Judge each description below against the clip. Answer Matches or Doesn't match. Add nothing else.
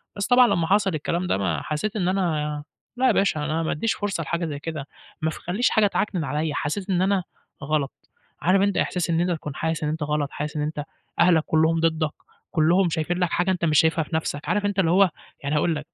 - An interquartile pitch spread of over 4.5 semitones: Doesn't match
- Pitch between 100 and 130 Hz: Doesn't match